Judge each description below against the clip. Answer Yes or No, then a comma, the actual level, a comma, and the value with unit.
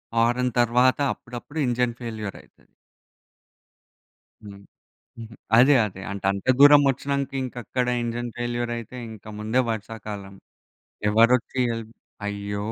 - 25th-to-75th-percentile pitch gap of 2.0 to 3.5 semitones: Yes, average, 2.8 semitones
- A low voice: Yes, low, 120 Hz